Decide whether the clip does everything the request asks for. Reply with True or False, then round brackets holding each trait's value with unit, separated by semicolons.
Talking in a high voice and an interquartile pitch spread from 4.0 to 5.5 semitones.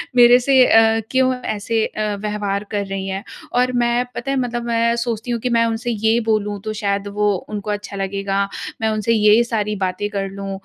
False (215 Hz; 2.8 semitones)